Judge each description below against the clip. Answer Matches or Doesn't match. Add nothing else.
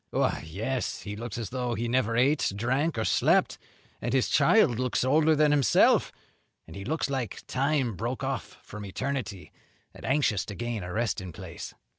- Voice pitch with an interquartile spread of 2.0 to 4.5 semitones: Matches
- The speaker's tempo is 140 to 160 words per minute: Doesn't match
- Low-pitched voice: Matches